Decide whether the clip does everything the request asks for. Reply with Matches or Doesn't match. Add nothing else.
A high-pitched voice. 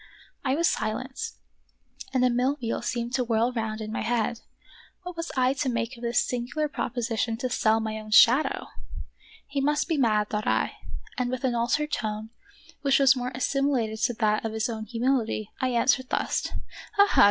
Matches